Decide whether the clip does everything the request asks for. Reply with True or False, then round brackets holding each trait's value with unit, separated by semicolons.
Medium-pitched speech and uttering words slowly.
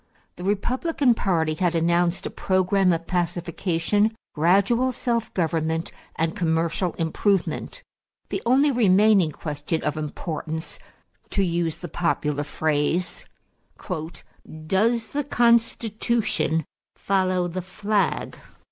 True (180 Hz; 105 wpm)